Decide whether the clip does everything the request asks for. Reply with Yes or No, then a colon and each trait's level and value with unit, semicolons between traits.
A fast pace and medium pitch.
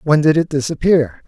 No: average, 190 wpm; medium, 150 Hz